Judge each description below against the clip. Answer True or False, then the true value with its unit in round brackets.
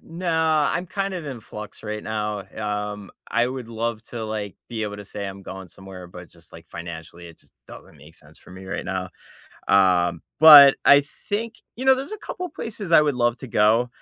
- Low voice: True (105 Hz)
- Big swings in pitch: True (7.4 semitones)